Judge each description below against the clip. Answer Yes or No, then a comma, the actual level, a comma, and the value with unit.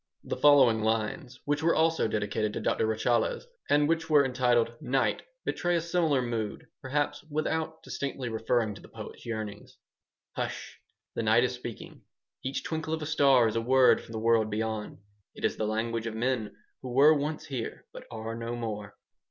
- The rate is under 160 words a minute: No, average, 180 wpm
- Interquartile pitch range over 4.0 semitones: Yes, average, 4.7 semitones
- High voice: No, low, 120 Hz